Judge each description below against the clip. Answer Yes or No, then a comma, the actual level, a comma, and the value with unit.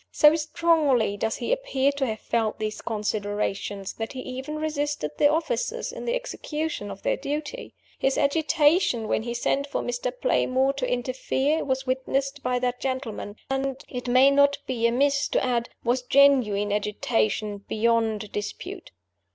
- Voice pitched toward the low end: No, very high, 260 Hz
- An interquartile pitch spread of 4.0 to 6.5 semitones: Yes, average, 4.3 semitones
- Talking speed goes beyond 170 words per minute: No, average, 155 wpm